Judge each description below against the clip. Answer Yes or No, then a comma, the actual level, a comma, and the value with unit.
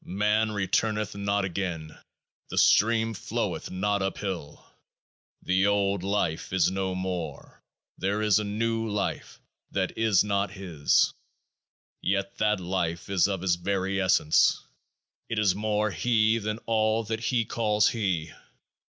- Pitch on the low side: Yes, low, 100 Hz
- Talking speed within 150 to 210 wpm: No, slow, 135 wpm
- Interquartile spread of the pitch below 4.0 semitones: Yes, narrow, 2.4 semitones